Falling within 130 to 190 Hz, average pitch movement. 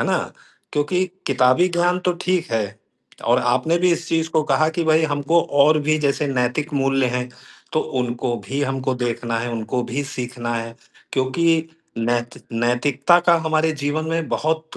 Yes: medium, 140 Hz; average, 4.6 semitones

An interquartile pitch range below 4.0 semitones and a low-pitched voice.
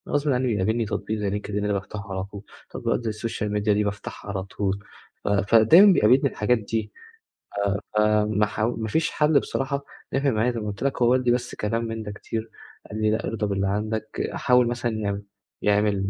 Yes: average, 2.7 semitones; low, 110 Hz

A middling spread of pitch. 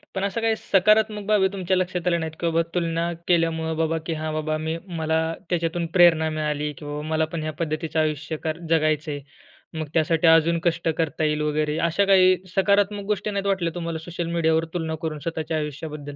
No: narrow, 2.2 semitones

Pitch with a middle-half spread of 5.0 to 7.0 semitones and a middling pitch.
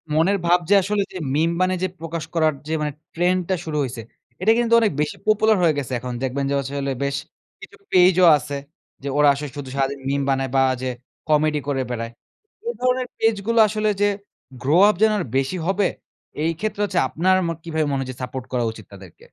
Yes: wide, 5.5 semitones; medium, 155 Hz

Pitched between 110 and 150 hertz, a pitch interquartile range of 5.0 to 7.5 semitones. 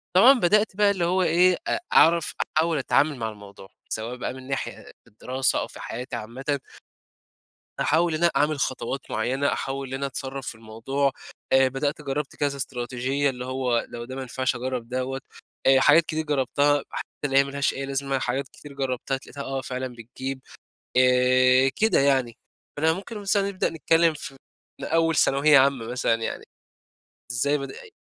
No: low, 135 Hz; average, 2.8 semitones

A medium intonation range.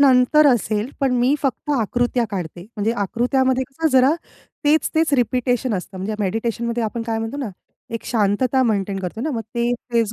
Yes: average, 3.2 semitones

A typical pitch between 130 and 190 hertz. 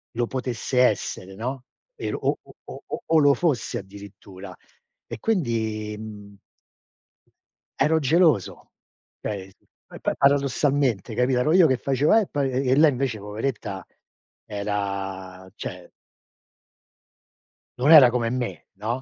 No: low, 120 Hz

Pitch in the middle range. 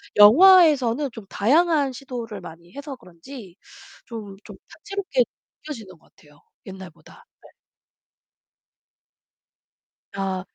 No: high, 225 Hz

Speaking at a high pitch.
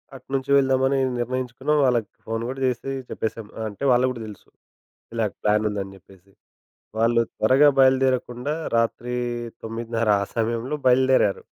No: low, 120 Hz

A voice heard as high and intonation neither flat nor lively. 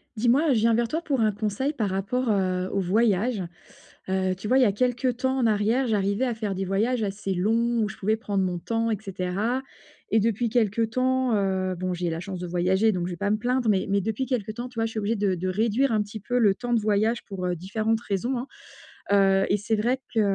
Yes: high, 215 Hz; average, 3.5 semitones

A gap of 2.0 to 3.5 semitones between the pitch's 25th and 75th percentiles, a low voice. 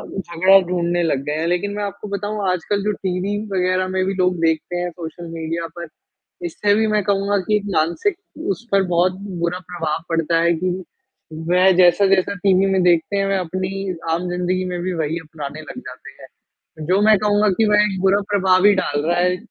No: narrow, 2.6 semitones; medium, 185 Hz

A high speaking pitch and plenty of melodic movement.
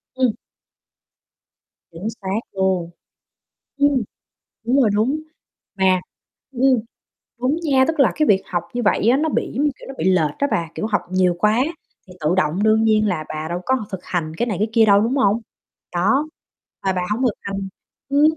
Yes: high, 215 Hz; wide, 5.7 semitones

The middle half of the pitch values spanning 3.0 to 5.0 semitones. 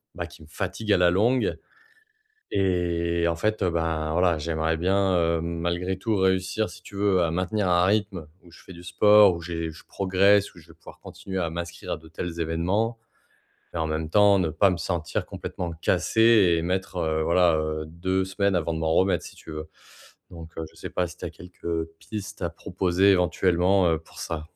No: narrow, 2.5 semitones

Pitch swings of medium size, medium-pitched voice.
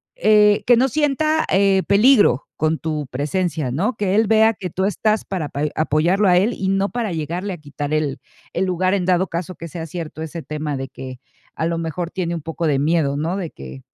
Yes: average, 4.4 semitones; medium, 175 Hz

